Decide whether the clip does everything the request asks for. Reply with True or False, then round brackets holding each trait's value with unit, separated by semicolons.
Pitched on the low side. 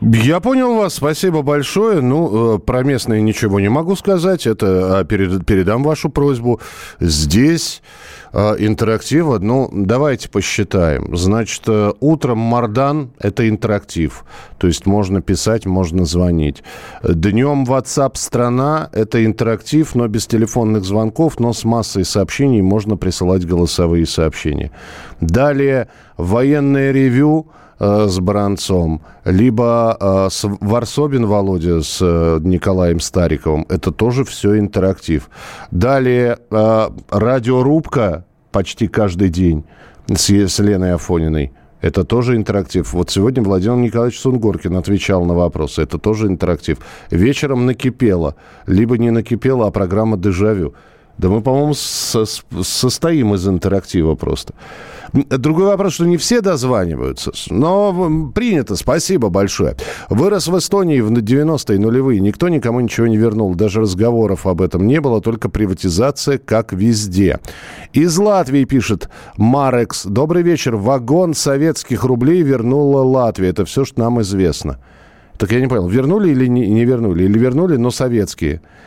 True (110 Hz)